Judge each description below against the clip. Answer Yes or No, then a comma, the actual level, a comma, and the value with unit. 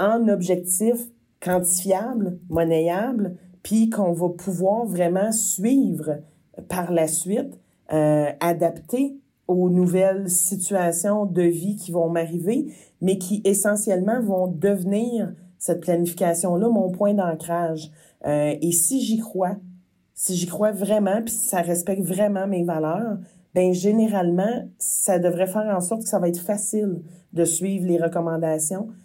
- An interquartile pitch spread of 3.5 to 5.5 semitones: No, average, 3.1 semitones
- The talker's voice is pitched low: No, medium, 185 Hz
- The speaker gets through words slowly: Yes, slow, 130 wpm